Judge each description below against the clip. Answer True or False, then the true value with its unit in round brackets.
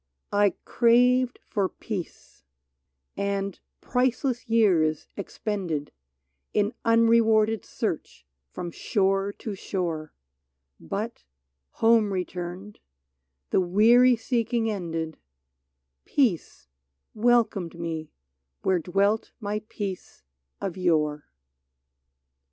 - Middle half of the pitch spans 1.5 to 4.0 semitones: False (4.5 semitones)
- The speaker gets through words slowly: True (85 wpm)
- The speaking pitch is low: False (200 Hz)